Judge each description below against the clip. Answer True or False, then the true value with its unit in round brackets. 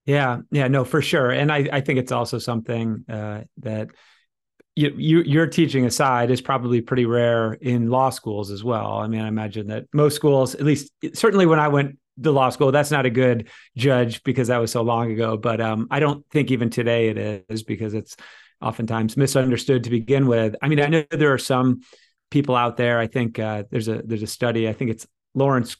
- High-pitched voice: False (125 Hz)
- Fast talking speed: True (215 wpm)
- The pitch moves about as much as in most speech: True (3.6 semitones)